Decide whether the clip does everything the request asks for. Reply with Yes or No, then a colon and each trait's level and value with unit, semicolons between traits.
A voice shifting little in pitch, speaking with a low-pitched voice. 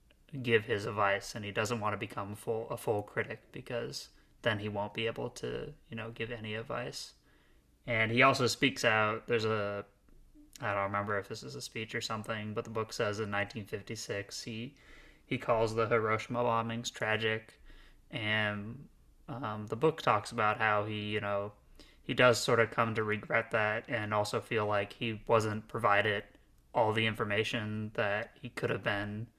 Yes: narrow, 2.0 semitones; low, 110 Hz